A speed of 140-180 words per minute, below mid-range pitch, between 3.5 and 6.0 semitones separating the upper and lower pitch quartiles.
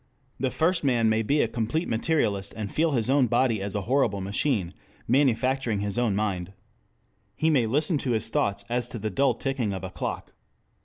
No: average, 195 wpm; low, 115 Hz; average, 4.9 semitones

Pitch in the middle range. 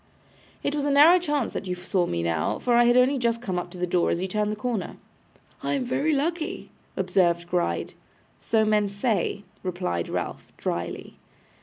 No: high, 210 Hz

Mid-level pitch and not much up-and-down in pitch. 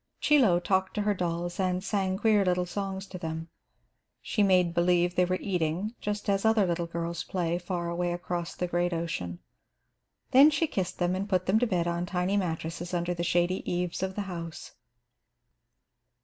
Yes: medium, 180 Hz; narrow, 2.0 semitones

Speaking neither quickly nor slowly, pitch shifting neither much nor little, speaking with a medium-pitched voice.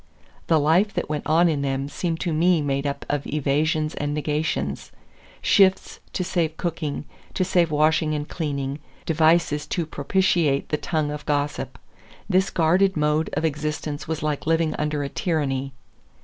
No: average, 160 wpm; narrow, 2.2 semitones; medium, 155 Hz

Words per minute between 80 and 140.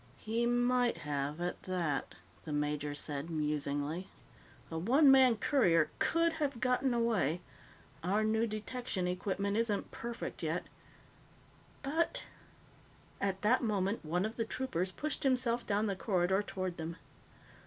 Yes: slow, 135 wpm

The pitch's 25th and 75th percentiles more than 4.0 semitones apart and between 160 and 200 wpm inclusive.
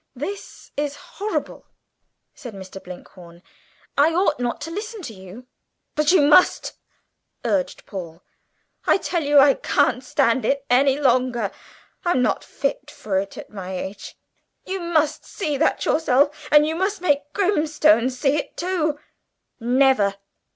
No: average, 5.0 semitones; average, 145 wpm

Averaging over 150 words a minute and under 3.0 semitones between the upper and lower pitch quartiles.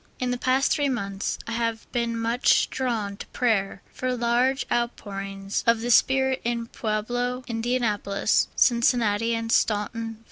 No: average, 145 wpm; narrow, 2.5 semitones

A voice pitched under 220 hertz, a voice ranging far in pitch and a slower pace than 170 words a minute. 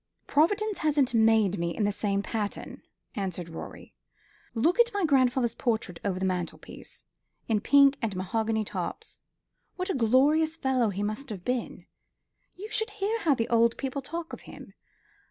No: high, 235 Hz; wide, 7.0 semitones; average, 160 wpm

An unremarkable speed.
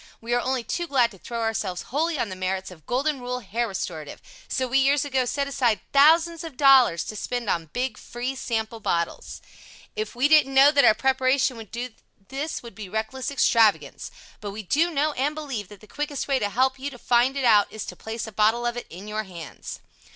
No: fast, 220 wpm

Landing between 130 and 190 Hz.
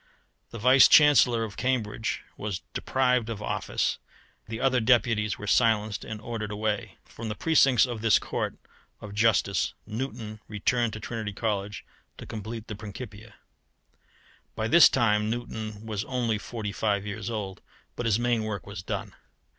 No: low, 110 Hz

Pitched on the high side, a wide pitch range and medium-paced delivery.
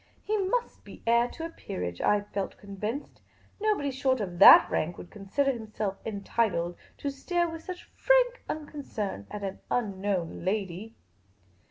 Yes: high, 220 Hz; wide, 7.1 semitones; average, 155 wpm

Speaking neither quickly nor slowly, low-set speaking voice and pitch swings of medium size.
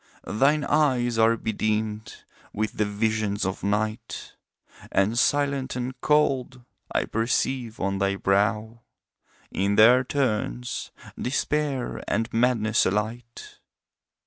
No: slow, 105 wpm; low, 115 Hz; average, 3.3 semitones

